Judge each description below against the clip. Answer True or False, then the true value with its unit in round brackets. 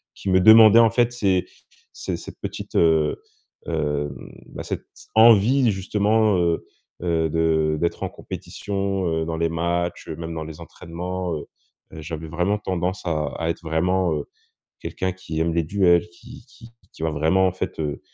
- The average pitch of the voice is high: False (85 Hz)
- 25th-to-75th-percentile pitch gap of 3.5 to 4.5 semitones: False (3.1 semitones)